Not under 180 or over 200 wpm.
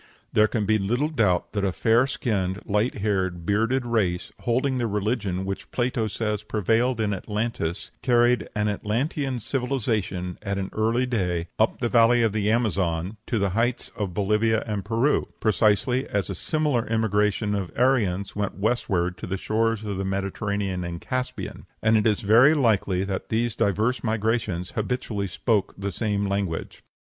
No: average, 165 wpm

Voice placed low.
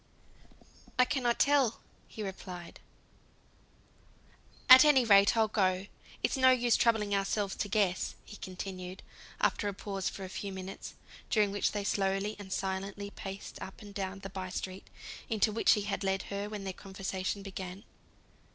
No: high, 200 Hz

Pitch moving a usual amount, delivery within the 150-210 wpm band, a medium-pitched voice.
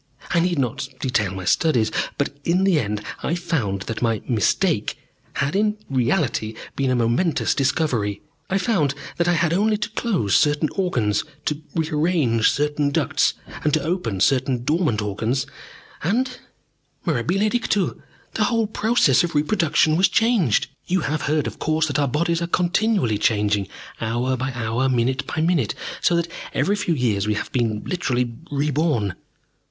No: wide, 6.7 semitones; average, 160 wpm; medium, 145 Hz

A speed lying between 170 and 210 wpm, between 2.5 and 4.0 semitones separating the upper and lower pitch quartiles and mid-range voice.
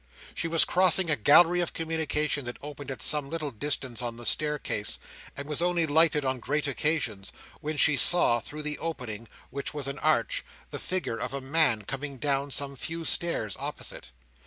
Yes: average, 180 wpm; average, 3.4 semitones; medium, 150 Hz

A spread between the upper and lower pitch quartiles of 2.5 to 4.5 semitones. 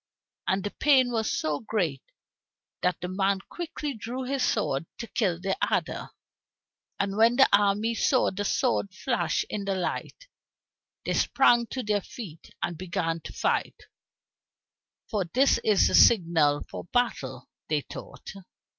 No: average, 5.1 semitones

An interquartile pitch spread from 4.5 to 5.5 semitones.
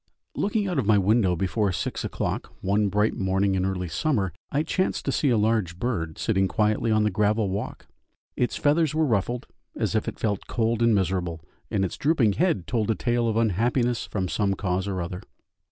No: average, 3.7 semitones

